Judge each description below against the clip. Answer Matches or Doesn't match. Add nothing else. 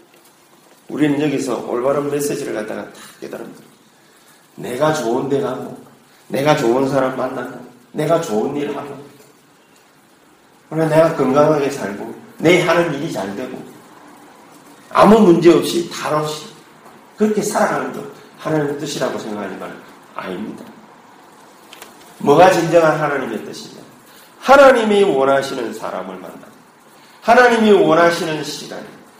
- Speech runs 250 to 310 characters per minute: Matches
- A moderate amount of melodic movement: Matches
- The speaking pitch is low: Doesn't match